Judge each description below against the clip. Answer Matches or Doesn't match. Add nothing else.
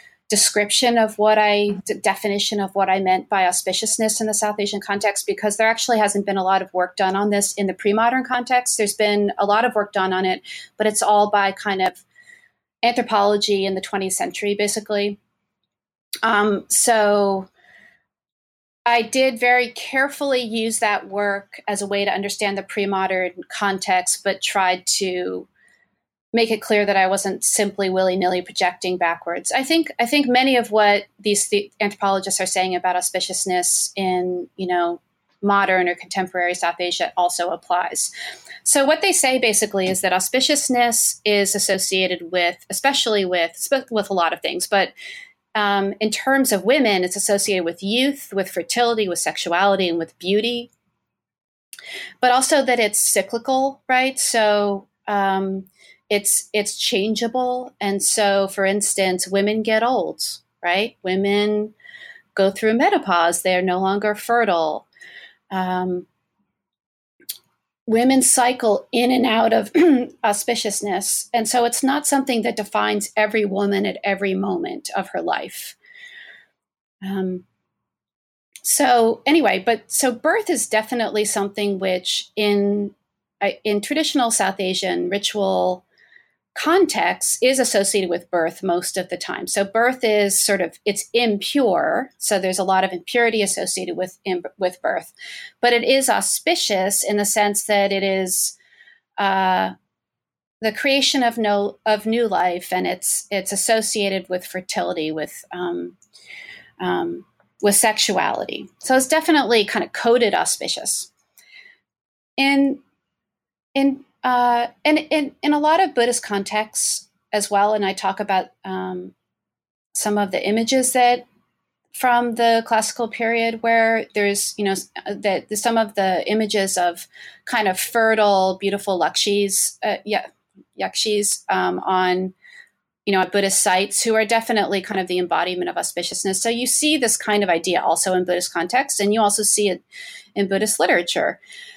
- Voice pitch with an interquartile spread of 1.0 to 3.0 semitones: Doesn't match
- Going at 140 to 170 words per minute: Matches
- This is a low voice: Doesn't match